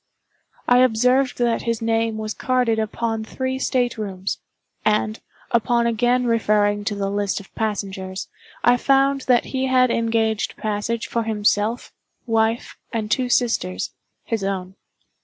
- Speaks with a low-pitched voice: No, high, 225 Hz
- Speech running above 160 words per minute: No, slow, 135 wpm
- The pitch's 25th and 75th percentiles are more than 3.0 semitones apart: No, narrow, 2.6 semitones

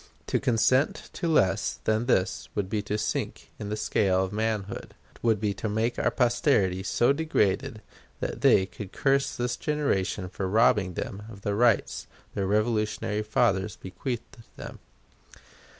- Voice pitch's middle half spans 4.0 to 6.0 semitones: No, average, 3.5 semitones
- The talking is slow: No, average, 150 wpm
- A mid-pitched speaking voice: No, low, 105 Hz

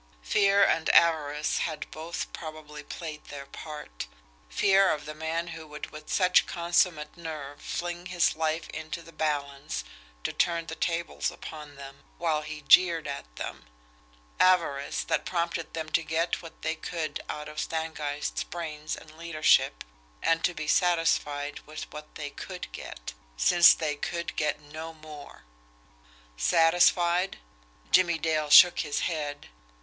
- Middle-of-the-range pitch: Yes, medium, 155 Hz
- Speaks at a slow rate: No, average, 145 wpm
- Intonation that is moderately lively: No, narrow, 2.2 semitones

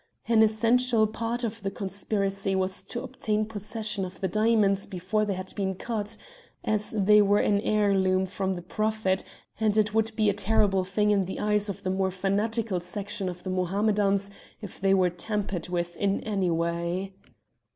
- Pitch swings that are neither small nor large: No, narrow, 2.1 semitones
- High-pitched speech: Yes, high, 200 Hz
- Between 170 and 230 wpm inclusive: Yes, average, 175 wpm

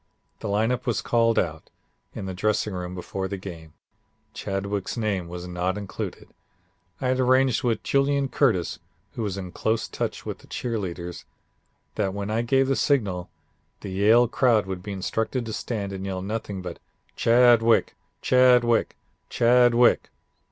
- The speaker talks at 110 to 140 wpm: No, average, 155 wpm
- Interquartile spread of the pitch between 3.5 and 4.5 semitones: Yes, average, 4.2 semitones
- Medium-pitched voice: No, low, 105 Hz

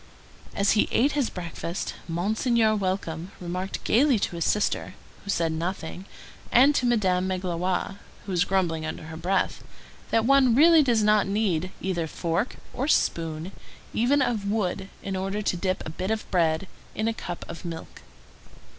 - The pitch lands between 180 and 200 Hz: Yes, high, 190 Hz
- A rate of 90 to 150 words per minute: No, average, 165 wpm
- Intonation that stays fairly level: No, average, 4.2 semitones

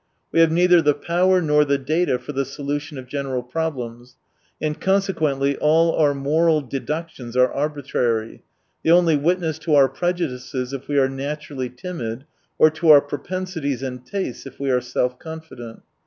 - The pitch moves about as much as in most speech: Yes, average, 3.8 semitones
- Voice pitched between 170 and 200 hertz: No, medium, 145 Hz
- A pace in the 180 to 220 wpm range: No, average, 170 wpm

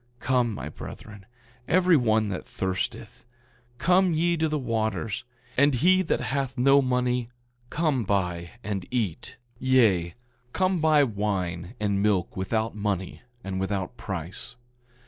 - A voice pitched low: Yes, low, 115 Hz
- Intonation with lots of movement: Yes, wide, 5.8 semitones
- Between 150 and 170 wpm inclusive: No, slow, 135 wpm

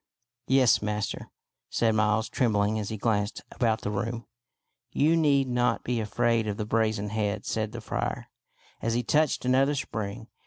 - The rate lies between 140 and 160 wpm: No, average, 170 wpm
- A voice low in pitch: Yes, low, 110 Hz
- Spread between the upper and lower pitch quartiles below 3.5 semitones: Yes, narrow, 2.6 semitones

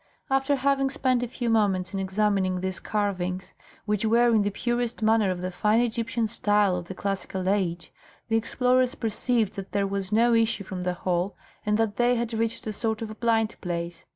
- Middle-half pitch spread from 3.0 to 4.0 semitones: Yes, average, 3.6 semitones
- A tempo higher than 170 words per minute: Yes, average, 195 wpm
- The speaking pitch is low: No, high, 215 Hz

